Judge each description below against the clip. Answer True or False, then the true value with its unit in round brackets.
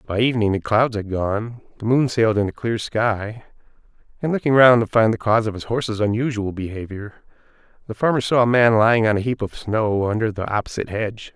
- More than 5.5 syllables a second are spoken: True (6.0 syllables/s)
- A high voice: False (110 Hz)